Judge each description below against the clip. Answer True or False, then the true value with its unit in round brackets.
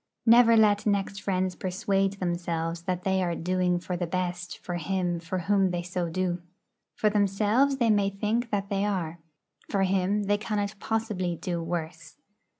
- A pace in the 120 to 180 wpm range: True (165 wpm)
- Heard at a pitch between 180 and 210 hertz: True (190 Hz)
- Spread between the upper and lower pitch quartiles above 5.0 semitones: False (2.7 semitones)